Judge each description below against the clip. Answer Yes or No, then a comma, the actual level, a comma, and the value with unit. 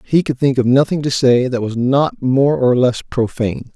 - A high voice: No, low, 130 Hz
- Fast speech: Yes, fast, 225 wpm